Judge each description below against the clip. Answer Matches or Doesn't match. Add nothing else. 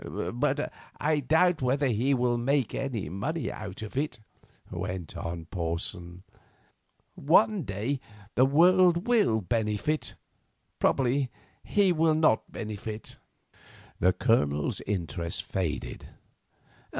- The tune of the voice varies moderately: Doesn't match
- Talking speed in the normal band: Doesn't match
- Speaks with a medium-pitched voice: Doesn't match